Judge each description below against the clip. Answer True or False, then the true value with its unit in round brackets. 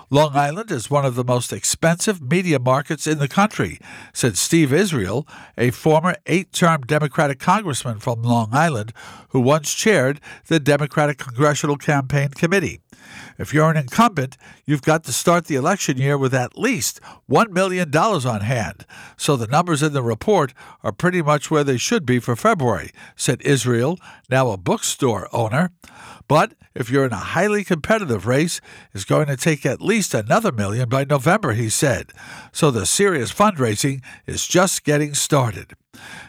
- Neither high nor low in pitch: True (145 Hz)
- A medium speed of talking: True (165 wpm)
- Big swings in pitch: False (4.4 semitones)